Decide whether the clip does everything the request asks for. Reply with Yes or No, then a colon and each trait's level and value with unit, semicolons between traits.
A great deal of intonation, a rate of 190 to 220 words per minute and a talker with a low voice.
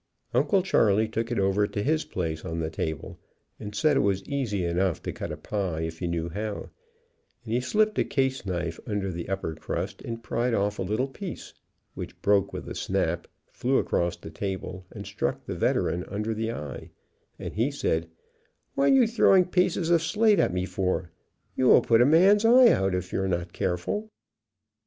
Yes: wide, 7.1 semitones; average, 195 wpm; low, 105 Hz